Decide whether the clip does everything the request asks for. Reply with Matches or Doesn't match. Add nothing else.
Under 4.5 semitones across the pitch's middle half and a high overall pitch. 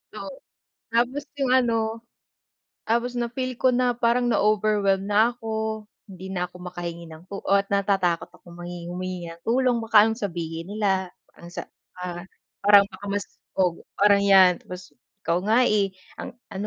Matches